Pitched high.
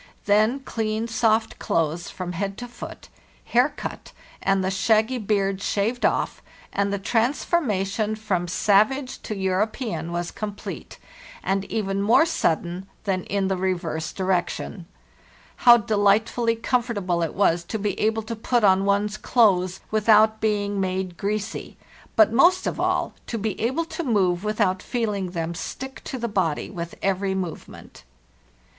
Yes: high, 205 Hz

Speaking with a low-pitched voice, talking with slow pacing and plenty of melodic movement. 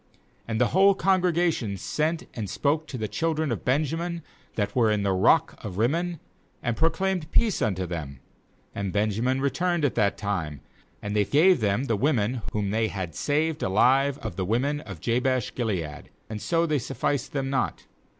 No: low, 125 Hz; average, 185 wpm; wide, 7.3 semitones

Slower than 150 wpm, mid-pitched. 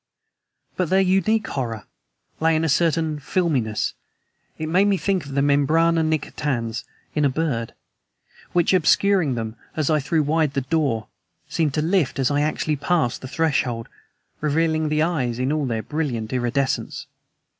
No: average, 155 wpm; medium, 150 Hz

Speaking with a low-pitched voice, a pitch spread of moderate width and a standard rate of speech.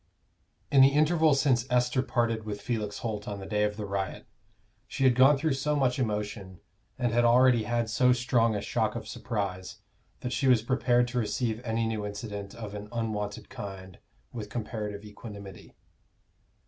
Yes: low, 115 Hz; average, 3.2 semitones; average, 175 wpm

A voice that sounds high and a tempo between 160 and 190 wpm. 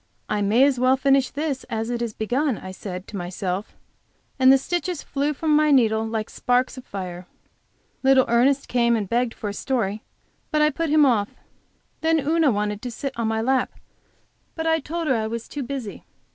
No: very high, 250 Hz; average, 200 wpm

